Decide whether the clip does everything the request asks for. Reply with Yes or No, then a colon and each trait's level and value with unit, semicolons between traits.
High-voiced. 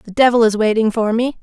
Yes: high, 225 Hz